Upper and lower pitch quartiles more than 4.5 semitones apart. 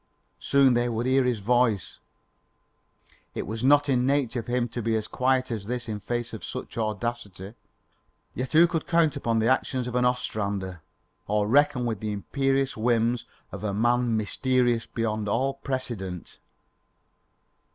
No: average, 3.0 semitones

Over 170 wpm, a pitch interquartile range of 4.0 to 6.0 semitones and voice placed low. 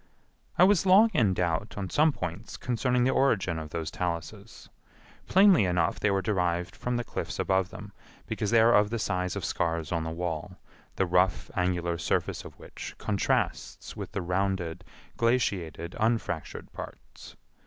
No: average, 165 wpm; average, 5.2 semitones; very low, 95 Hz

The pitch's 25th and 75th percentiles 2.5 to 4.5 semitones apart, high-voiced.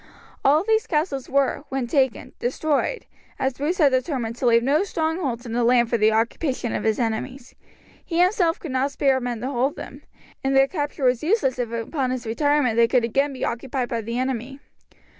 Yes: average, 3.4 semitones; very high, 260 Hz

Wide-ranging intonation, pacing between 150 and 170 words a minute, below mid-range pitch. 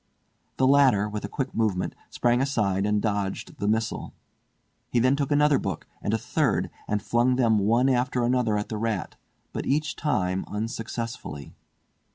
No: average, 3.7 semitones; average, 165 wpm; low, 115 Hz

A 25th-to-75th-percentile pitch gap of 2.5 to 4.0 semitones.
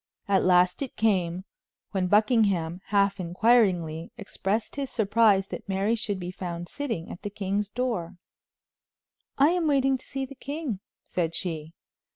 No: average, 4.5 semitones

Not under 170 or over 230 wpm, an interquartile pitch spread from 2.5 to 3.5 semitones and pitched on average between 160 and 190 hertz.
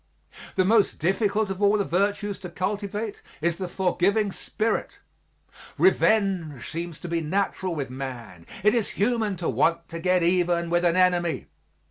No: average, 155 wpm; average, 3.2 semitones; medium, 185 Hz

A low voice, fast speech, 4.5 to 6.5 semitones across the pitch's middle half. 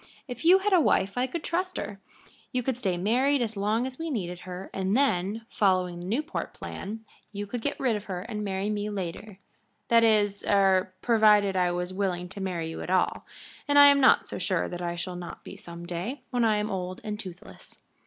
No: high, 205 Hz; fast, 220 wpm; average, 4.8 semitones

